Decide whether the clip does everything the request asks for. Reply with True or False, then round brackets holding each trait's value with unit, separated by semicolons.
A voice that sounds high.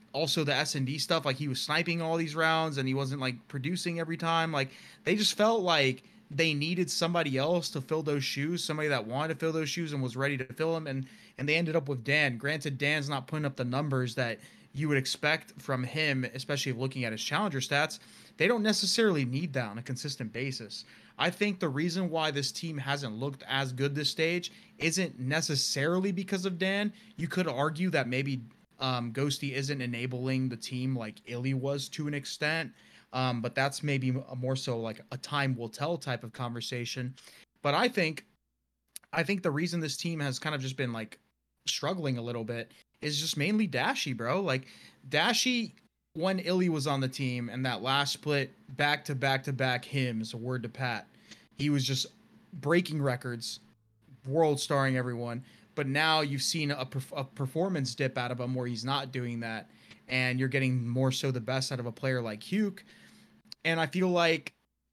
False (140 Hz)